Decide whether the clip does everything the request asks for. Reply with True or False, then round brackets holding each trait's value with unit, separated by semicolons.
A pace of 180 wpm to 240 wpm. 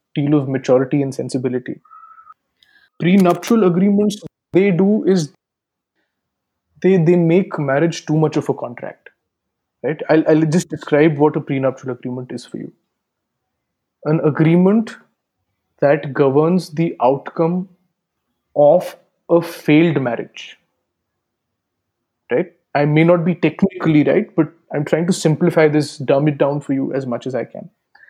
False (135 wpm)